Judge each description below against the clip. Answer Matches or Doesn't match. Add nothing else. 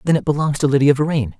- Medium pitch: Matches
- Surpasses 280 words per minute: Doesn't match